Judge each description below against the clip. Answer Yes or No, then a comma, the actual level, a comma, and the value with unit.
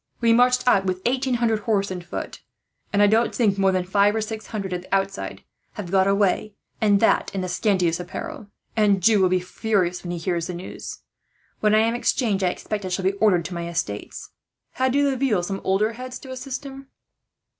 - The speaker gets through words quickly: Yes, fast, 215 wpm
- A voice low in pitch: No, high, 200 Hz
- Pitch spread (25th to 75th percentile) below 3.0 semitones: No, average, 3.6 semitones